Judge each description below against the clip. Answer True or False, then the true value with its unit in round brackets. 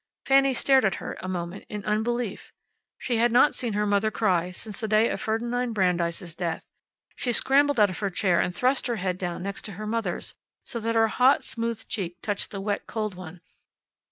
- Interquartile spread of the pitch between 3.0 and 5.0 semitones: True (4.1 semitones)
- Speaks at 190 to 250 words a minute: True (200 wpm)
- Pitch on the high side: True (215 Hz)